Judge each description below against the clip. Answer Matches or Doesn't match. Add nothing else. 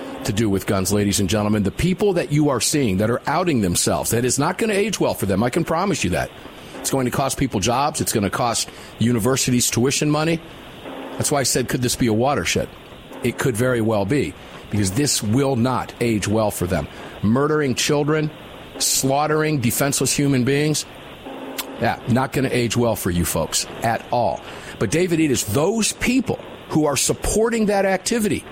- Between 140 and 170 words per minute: Doesn't match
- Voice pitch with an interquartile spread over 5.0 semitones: Matches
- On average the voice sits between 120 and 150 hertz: Matches